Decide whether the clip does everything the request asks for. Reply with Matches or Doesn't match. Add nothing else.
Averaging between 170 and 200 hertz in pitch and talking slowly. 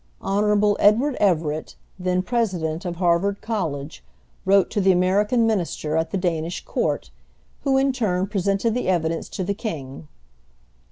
Doesn't match